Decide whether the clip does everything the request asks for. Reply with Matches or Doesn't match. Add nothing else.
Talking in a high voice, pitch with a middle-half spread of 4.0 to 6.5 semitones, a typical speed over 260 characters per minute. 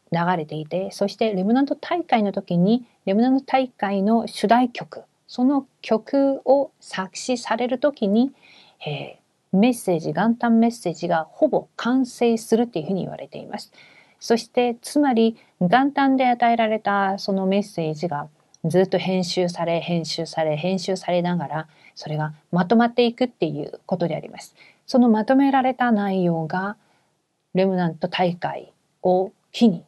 Matches